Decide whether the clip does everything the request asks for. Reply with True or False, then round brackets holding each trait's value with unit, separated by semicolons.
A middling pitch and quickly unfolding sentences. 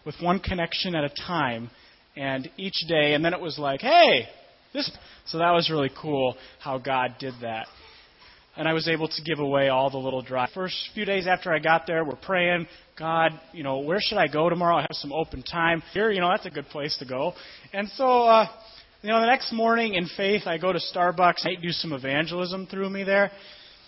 True (165 Hz; 220 wpm)